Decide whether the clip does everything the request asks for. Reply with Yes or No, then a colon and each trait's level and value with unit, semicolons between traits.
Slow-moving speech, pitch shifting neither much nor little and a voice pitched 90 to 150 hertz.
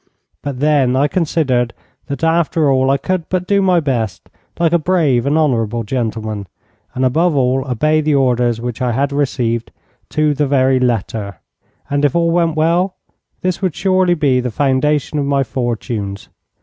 No: average, 170 wpm; average, 4.5 semitones; medium, 140 Hz